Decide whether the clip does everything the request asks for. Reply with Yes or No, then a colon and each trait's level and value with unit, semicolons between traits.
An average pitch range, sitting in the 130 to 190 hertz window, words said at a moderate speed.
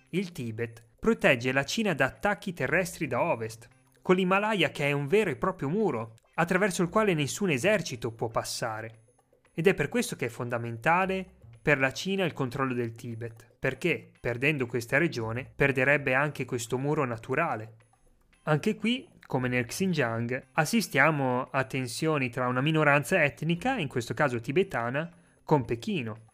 No: wide, 6.5 semitones; medium, 140 Hz; average, 155 wpm